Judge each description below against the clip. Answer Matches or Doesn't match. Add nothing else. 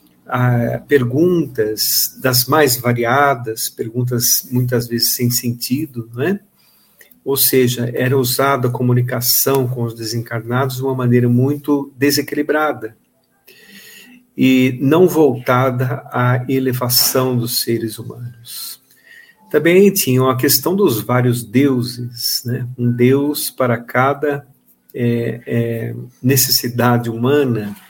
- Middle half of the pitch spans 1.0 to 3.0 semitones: Matches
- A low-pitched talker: Matches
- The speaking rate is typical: Doesn't match